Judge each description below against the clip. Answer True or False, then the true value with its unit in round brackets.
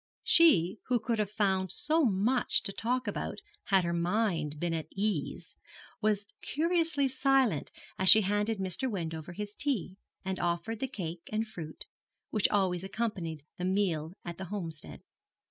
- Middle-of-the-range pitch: False (195 Hz)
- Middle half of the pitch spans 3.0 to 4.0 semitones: False (4.7 semitones)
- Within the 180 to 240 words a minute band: False (155 wpm)